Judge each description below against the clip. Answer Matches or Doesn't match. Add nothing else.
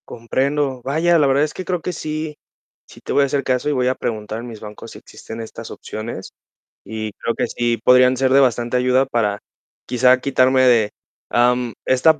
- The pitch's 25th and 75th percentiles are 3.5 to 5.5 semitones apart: Doesn't match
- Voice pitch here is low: Matches